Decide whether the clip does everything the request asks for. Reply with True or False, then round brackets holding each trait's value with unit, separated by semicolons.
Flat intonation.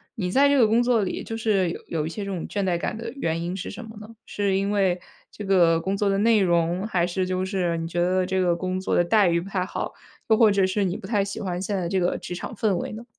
False (3.0 semitones)